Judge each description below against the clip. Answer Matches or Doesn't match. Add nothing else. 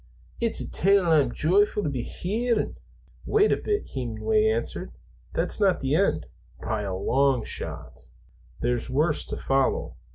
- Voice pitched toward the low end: Doesn't match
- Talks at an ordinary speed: Matches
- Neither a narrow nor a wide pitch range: Doesn't match